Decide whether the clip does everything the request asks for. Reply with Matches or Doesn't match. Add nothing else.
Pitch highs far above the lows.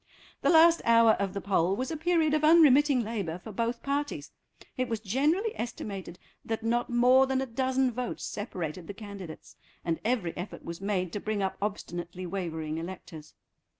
Matches